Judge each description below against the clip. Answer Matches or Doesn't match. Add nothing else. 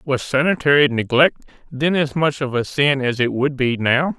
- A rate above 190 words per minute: Matches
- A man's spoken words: Matches